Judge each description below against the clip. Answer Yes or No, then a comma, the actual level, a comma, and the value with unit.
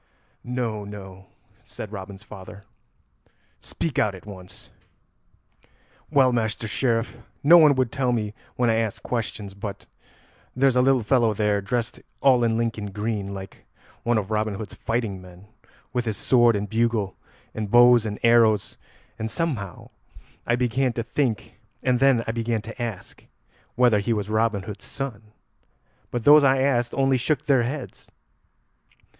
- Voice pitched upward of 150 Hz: No, low, 115 Hz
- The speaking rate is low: No, average, 150 wpm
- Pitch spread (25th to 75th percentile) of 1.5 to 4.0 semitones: Yes, average, 3.2 semitones